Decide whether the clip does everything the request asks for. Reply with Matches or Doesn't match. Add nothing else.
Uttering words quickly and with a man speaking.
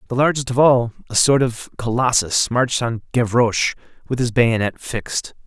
Doesn't match